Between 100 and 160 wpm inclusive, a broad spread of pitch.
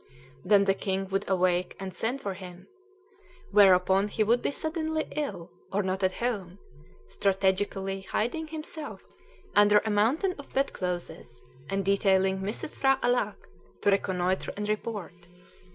No: slow, 135 wpm; average, 3.5 semitones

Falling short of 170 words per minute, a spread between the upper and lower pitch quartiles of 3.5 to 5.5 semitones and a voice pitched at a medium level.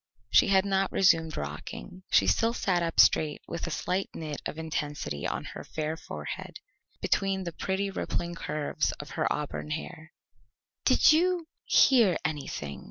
Yes: average, 155 wpm; average, 4.3 semitones; medium, 165 Hz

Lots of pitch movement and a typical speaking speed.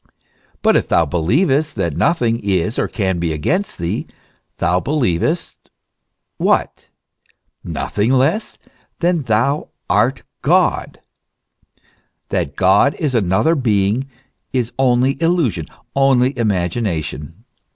No: wide, 6.9 semitones; slow, 110 wpm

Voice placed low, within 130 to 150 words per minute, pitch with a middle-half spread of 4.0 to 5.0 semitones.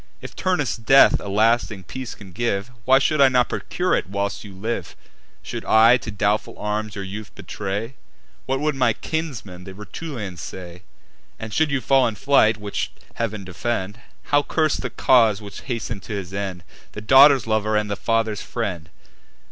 No: low, 110 Hz; average, 175 wpm; average, 4.4 semitones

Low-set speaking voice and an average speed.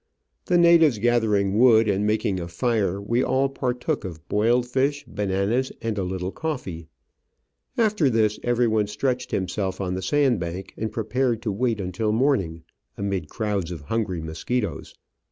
Yes: low, 110 Hz; average, 155 wpm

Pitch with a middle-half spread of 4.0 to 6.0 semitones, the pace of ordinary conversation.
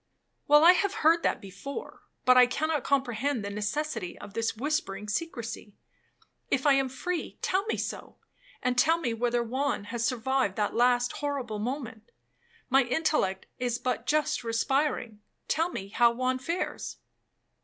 Yes: average, 4.6 semitones; average, 150 wpm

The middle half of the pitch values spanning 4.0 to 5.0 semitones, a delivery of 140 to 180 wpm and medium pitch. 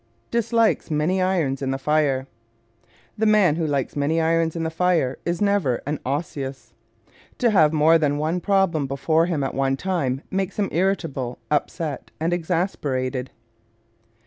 Yes: average, 4.7 semitones; average, 155 wpm; medium, 160 Hz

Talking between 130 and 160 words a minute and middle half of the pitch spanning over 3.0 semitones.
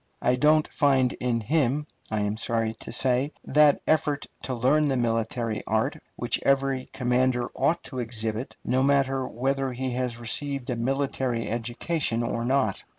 No: average, 155 wpm; average, 2.7 semitones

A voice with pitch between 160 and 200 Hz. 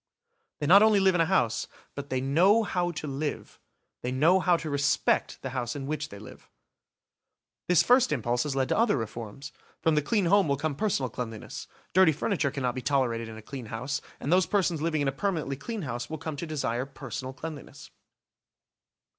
No: medium, 145 Hz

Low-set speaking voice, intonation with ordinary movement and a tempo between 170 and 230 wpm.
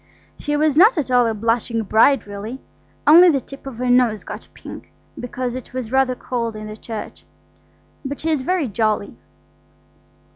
No: very high, 250 Hz; average, 3.6 semitones; average, 175 wpm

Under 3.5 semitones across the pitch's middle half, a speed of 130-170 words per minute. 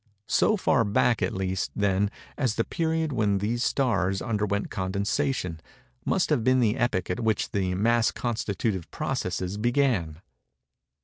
No: average, 4.4 semitones; average, 140 wpm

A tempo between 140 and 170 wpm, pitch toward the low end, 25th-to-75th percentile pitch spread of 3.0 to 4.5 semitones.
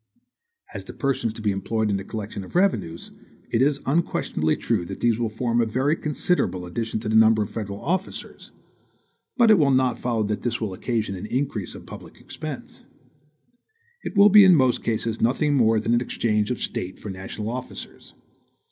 No: average, 190 wpm; low, 115 Hz; average, 4.0 semitones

